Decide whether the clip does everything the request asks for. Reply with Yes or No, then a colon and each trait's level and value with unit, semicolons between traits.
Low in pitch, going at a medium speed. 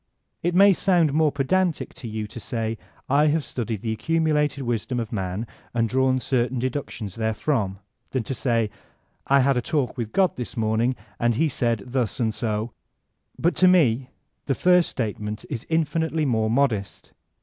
Yes: low, 125 Hz; average, 170 wpm